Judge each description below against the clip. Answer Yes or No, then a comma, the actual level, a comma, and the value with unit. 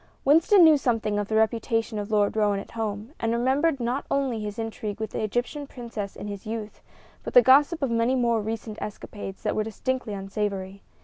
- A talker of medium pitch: No, high, 225 Hz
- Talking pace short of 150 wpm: No, average, 195 wpm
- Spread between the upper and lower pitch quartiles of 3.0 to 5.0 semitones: Yes, average, 3.7 semitones